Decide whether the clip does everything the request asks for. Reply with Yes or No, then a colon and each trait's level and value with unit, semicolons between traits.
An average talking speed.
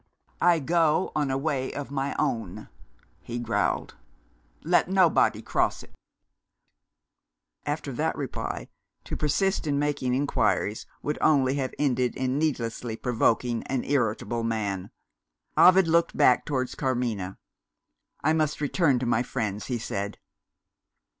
No: slow, 125 wpm